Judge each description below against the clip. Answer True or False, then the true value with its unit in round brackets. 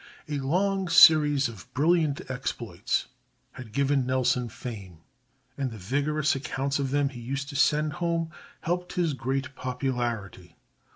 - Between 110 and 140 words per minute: True (135 wpm)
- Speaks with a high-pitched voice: False (135 Hz)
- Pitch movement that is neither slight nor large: True (3.3 semitones)